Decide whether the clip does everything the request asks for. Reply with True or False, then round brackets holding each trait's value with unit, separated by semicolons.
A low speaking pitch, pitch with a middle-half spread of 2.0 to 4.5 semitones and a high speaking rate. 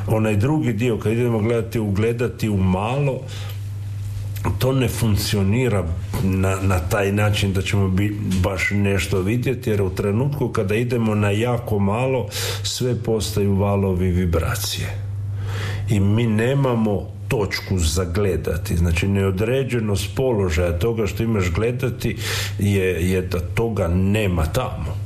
False (100 Hz; 2.8 semitones; 125 wpm)